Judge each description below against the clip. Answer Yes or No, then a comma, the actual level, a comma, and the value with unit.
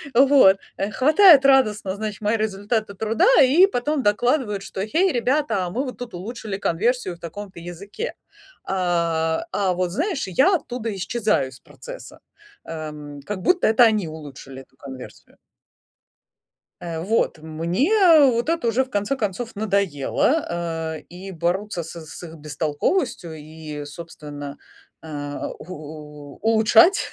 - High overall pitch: Yes, high, 200 Hz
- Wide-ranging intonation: Yes, wide, 7.0 semitones